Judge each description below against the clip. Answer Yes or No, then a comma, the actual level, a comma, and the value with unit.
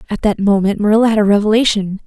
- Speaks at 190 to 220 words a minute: Yes, fast, 205 wpm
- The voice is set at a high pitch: Yes, high, 210 Hz